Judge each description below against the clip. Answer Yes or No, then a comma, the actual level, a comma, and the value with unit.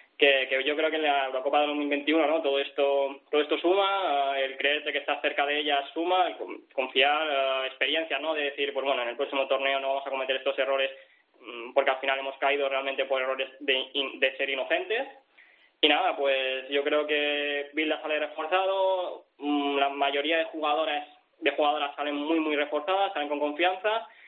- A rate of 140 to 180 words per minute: No, fast, 190 wpm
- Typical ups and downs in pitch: No, narrow, 1.8 semitones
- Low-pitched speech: No, medium, 145 Hz